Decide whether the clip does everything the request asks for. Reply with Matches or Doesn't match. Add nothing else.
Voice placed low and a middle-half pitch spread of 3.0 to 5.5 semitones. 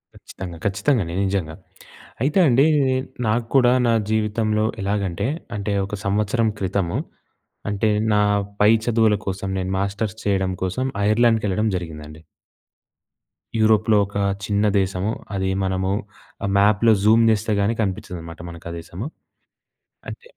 Doesn't match